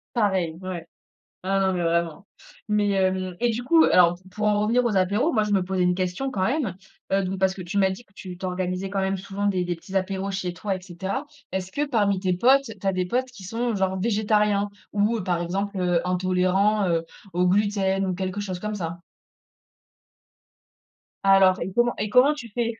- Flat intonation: Yes, narrow, 2.3 semitones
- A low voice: No, high, 195 Hz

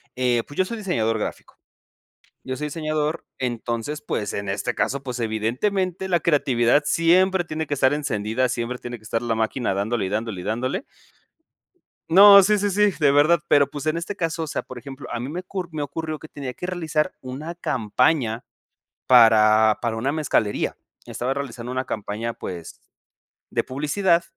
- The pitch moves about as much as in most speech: No, wide, 5.9 semitones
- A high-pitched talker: No, low, 135 Hz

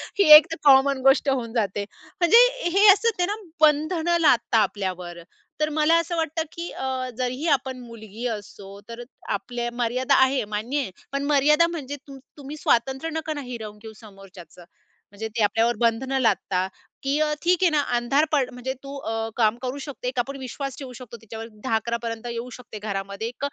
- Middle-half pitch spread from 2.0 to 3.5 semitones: No, average, 4.4 semitones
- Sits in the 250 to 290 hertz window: Yes, very high, 255 Hz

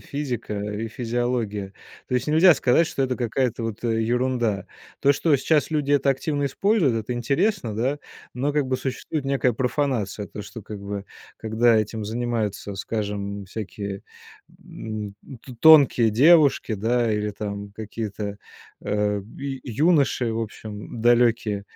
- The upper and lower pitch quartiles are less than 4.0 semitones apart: No, average, 4.4 semitones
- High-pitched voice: No, low, 115 Hz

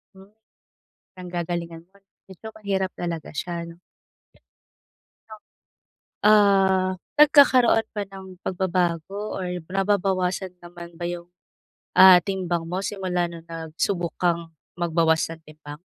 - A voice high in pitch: No, medium, 180 Hz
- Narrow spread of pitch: Yes, narrow, 2.2 semitones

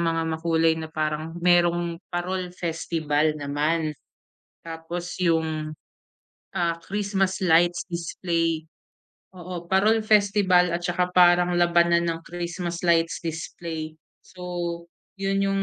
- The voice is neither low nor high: Yes, medium, 170 Hz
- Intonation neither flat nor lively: No, narrow, 1.6 semitones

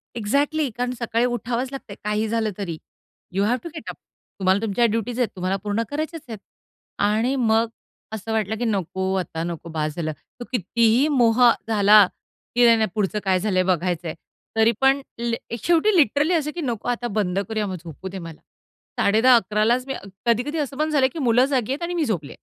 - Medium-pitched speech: No, high, 225 Hz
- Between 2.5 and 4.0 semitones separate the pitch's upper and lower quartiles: No, average, 4.5 semitones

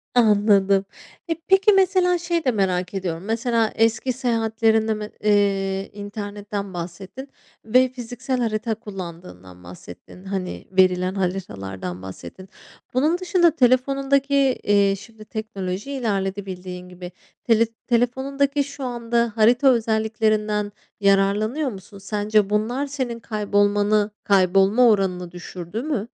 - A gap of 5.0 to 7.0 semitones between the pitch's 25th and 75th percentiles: No, average, 4.1 semitones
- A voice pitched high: Yes, high, 215 Hz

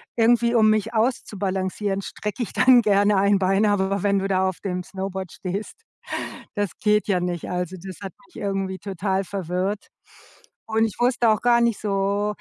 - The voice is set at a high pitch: Yes, high, 200 Hz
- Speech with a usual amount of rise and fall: No, narrow, 2.2 semitones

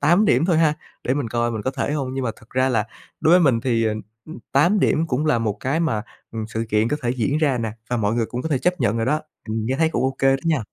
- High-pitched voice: No, low, 130 Hz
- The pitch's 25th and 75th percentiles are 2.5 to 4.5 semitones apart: No, average, 4.9 semitones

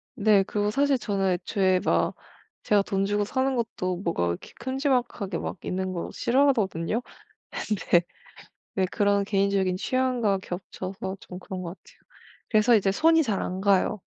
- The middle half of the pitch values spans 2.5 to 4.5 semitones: Yes, average, 4.0 semitones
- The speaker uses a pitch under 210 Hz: Yes, high, 200 Hz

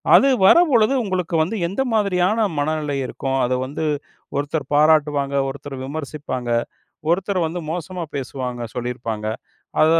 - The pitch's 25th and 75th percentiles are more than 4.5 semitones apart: Yes, average, 5.0 semitones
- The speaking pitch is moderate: Yes, medium, 155 Hz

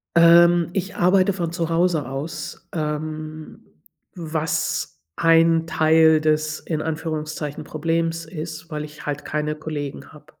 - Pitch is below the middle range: No, medium, 160 Hz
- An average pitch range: No, narrow, 1.5 semitones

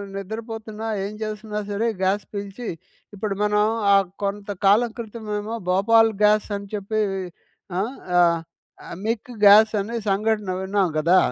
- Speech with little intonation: Yes, narrow, 1.9 semitones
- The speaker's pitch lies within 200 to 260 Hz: Yes, high, 210 Hz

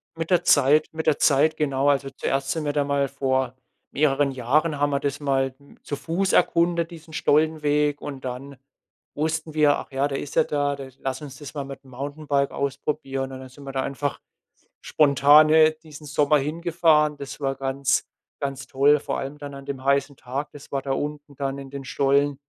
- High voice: No, medium, 140 Hz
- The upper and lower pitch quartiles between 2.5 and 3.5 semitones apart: No, narrow, 1.8 semitones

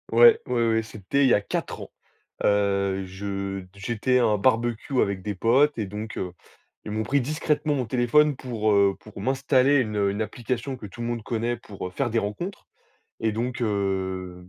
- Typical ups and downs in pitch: Yes, average, 4.2 semitones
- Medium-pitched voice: No, low, 110 Hz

